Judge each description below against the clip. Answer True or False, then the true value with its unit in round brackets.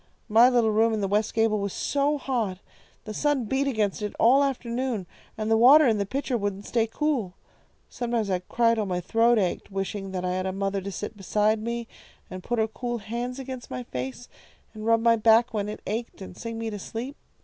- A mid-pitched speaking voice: False (225 Hz)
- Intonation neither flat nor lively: True (3.1 semitones)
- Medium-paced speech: False (215 wpm)